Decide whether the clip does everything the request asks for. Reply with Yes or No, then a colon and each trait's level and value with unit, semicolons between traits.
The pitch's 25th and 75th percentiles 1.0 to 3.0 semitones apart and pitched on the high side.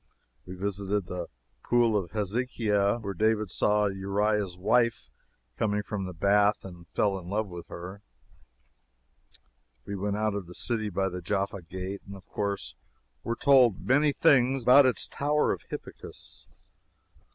No: narrow, 2.6 semitones; low, 100 Hz